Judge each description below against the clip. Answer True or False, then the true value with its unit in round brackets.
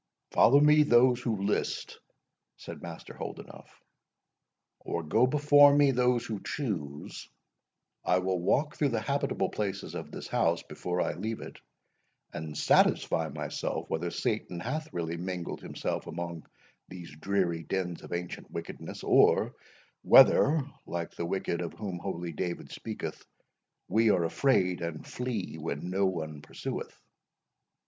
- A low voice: True (95 Hz)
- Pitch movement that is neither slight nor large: False (6.4 semitones)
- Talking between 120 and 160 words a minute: True (140 wpm)